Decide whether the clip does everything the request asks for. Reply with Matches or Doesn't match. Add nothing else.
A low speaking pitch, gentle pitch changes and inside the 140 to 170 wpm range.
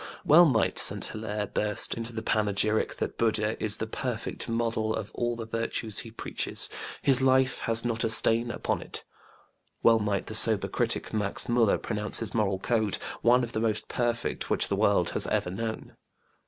Doesn't match